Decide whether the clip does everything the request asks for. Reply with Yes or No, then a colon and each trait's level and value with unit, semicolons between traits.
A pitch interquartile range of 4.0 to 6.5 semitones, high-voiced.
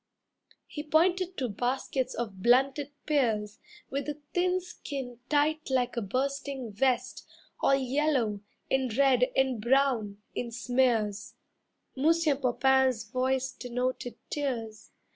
No: average, 2.7 semitones; very high, 260 Hz